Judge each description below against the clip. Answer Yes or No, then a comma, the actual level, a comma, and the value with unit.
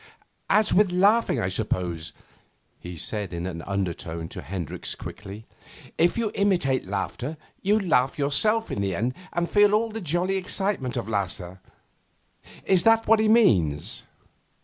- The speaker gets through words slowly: No, average, 150 wpm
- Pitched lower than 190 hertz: Yes, low, 135 Hz